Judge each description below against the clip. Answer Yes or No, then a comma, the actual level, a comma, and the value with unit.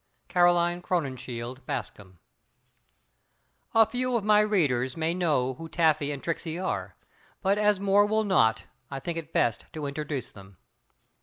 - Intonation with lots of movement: Yes, wide, 6.7 semitones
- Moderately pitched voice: Yes, medium, 165 Hz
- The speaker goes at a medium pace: Yes, average, 145 wpm